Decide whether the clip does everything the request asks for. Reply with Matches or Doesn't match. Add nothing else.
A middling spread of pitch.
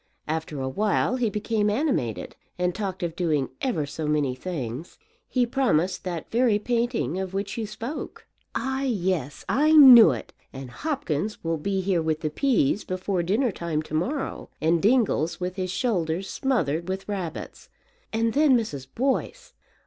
Doesn't match